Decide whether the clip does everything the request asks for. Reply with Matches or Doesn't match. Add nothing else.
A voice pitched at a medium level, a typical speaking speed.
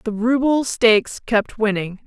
Doesn't match